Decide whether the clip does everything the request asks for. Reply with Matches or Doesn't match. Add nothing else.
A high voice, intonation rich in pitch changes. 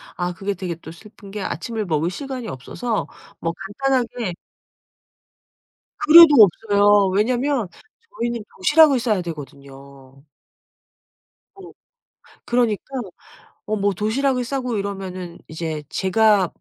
Matches